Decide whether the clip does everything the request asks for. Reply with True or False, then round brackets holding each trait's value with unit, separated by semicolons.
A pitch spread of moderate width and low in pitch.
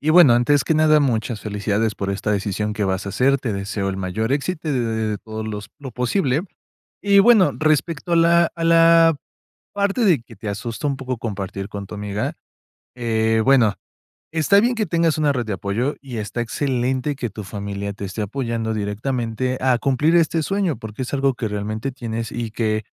False (6.0 semitones; 120 Hz)